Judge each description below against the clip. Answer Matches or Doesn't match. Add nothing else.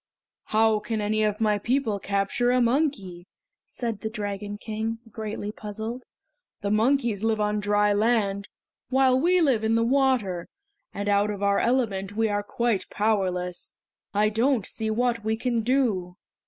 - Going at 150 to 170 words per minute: Matches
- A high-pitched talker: Matches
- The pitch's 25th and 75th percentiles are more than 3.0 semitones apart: Doesn't match